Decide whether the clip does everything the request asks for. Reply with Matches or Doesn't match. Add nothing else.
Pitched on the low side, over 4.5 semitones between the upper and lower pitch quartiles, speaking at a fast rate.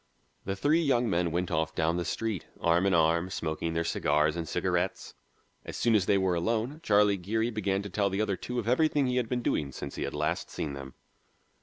Matches